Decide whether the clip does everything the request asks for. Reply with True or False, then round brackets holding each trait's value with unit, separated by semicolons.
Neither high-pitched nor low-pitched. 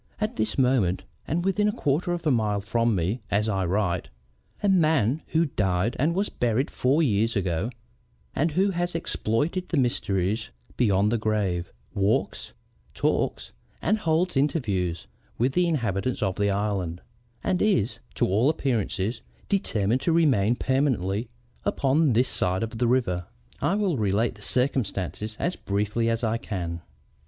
False (115 Hz)